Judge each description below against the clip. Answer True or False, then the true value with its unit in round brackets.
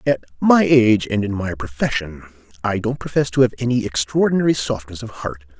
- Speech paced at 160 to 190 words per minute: True (180 wpm)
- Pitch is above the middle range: False (115 Hz)